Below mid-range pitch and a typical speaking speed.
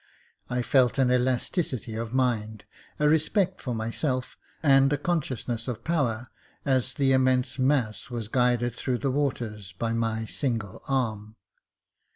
Yes: low, 125 Hz; average, 145 wpm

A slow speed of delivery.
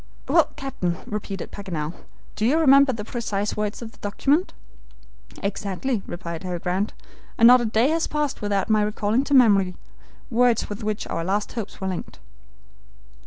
No: average, 165 wpm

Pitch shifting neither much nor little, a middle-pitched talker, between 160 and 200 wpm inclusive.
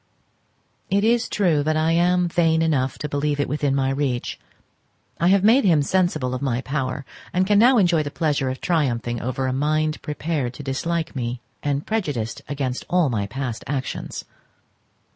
Yes: average, 4.4 semitones; medium, 145 Hz; average, 175 wpm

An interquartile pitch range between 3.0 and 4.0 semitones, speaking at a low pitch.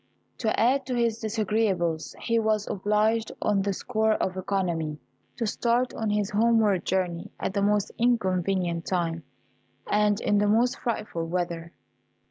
No: average, 3.4 semitones; high, 205 Hz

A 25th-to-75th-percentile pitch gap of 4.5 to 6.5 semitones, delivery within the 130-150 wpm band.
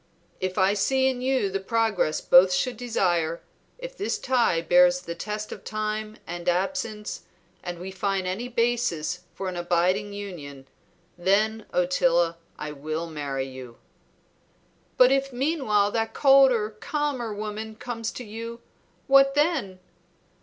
Yes: wide, 5.4 semitones; average, 140 wpm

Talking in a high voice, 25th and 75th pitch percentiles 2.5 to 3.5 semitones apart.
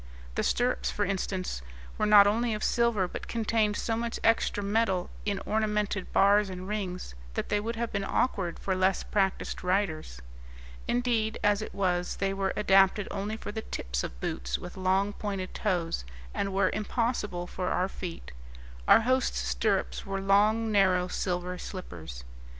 Yes: high, 195 Hz; average, 2.8 semitones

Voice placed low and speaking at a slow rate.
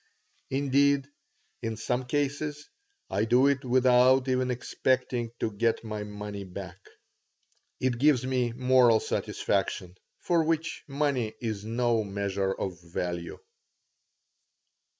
Yes: low, 125 Hz; slow, 110 wpm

